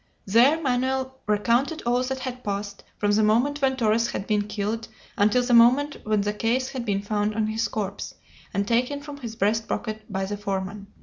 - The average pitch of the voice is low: No, high, 225 Hz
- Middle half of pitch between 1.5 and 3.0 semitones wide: No, average, 3.6 semitones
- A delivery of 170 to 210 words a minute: Yes, average, 195 wpm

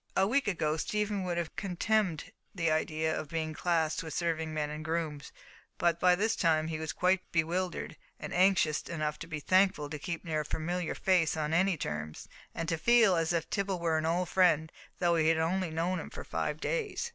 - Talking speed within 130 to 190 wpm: No, fast, 205 wpm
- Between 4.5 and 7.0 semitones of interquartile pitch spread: No, average, 2.7 semitones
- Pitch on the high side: No, medium, 165 Hz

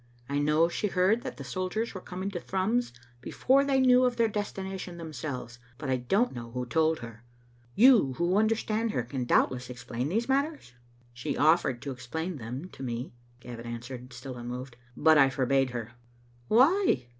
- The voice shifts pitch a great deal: Yes, wide, 8.8 semitones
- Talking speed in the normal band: Yes, average, 180 wpm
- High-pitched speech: No, medium, 155 Hz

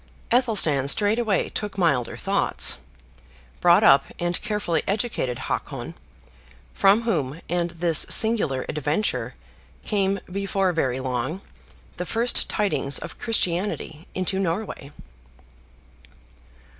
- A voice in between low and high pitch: Yes, medium, 180 Hz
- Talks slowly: Yes, slow, 100 wpm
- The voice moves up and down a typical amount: No, wide, 5.7 semitones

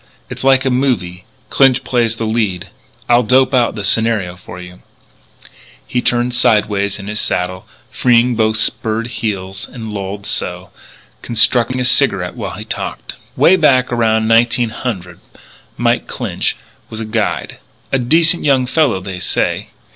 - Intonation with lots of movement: No, average, 3.7 semitones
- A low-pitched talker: Yes, low, 115 Hz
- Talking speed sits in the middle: Yes, average, 150 wpm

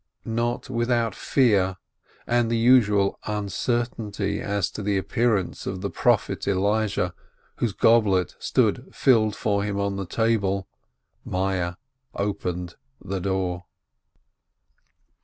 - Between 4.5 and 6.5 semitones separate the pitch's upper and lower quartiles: No, average, 3.2 semitones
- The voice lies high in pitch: No, low, 100 Hz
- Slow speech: Yes, slow, 110 wpm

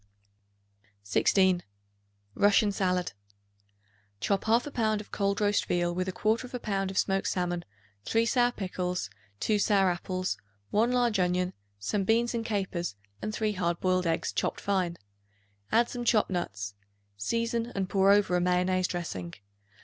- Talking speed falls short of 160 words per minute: Yes, average, 140 wpm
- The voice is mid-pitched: No, high, 195 Hz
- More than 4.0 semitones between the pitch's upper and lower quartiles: No, average, 3.3 semitones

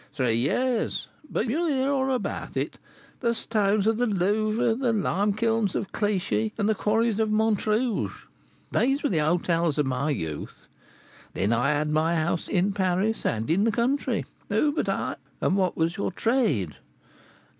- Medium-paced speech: Yes, average, 175 wpm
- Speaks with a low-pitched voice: No, high, 210 Hz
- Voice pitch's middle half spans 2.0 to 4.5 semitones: No, wide, 5.5 semitones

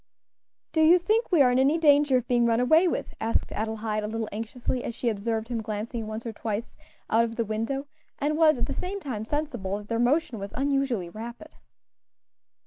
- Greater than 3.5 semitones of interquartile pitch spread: Yes, average, 4.5 semitones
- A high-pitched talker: Yes, high, 235 Hz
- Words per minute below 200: No, fast, 205 wpm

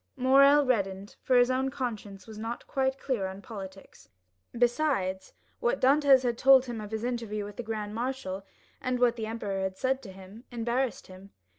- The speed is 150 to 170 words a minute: No, average, 180 wpm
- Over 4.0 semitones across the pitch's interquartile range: Yes, average, 4.5 semitones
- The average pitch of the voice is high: Yes, high, 235 Hz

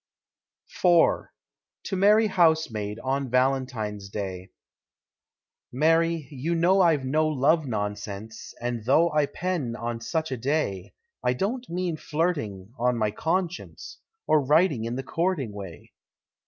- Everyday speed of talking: No, slow, 125 wpm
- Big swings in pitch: Yes, wide, 6.6 semitones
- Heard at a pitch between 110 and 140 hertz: Yes, low, 135 Hz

